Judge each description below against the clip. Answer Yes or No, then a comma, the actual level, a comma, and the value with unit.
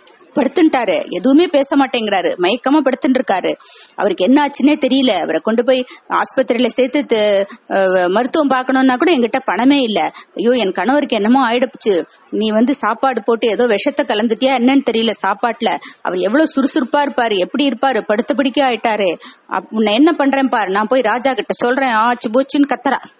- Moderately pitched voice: No, very high, 255 Hz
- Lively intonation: No, average, 3.8 semitones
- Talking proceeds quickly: Yes, fast, 145 wpm